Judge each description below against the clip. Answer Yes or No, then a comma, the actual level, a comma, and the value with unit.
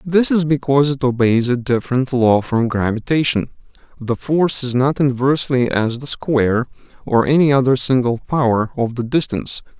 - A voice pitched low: Yes, low, 130 Hz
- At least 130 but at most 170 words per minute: Yes, average, 155 wpm